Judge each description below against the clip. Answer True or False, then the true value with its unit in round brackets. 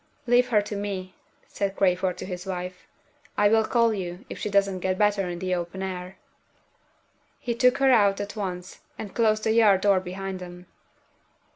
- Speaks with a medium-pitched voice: False (195 Hz)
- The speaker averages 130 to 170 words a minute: False (180 wpm)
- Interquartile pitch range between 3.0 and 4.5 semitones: False (2.5 semitones)